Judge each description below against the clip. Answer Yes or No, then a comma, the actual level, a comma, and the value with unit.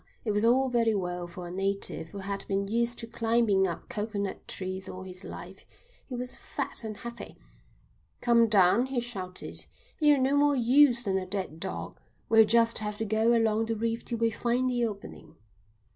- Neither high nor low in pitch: No, high, 225 Hz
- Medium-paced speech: Yes, average, 190 wpm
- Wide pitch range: No, average, 3.3 semitones